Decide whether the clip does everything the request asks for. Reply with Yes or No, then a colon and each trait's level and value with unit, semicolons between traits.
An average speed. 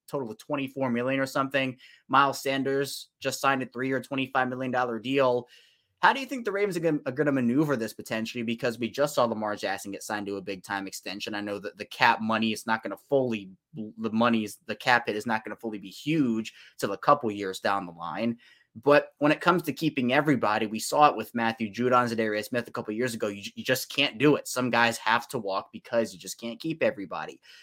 No: fast, 235 wpm